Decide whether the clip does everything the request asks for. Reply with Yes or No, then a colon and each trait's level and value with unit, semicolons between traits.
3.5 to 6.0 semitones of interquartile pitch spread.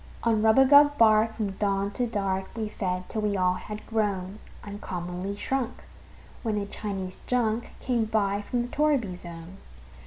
No: average, 3.0 semitones